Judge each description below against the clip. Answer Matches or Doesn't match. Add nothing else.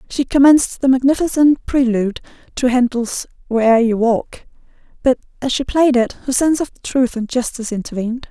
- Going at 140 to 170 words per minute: Matches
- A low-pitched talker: Doesn't match